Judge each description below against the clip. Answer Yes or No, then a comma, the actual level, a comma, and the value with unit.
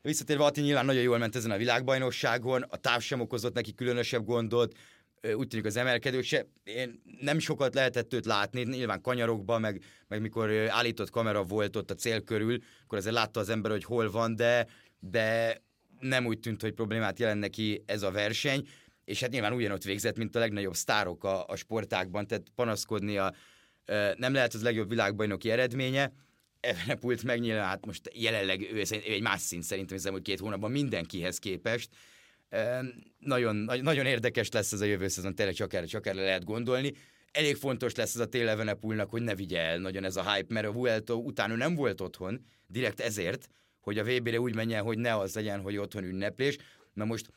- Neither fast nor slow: No, fast, 185 wpm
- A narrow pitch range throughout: No, average, 3.0 semitones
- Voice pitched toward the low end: Yes, low, 115 Hz